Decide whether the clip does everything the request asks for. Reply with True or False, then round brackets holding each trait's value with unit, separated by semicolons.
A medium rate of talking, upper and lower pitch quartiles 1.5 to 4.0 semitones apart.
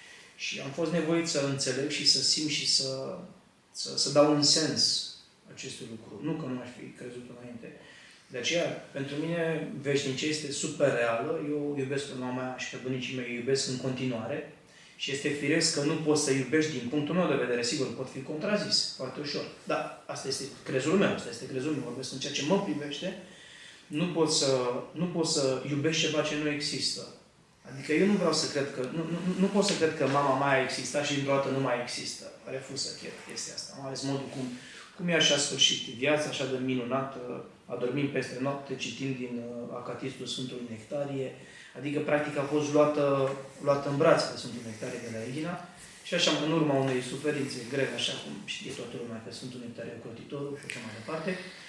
False (200 wpm; 2.9 semitones)